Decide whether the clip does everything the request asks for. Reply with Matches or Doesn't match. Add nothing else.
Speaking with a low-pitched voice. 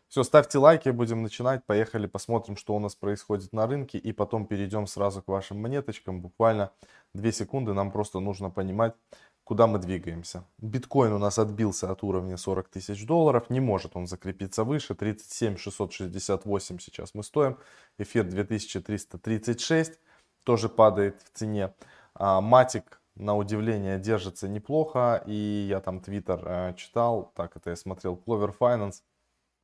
Matches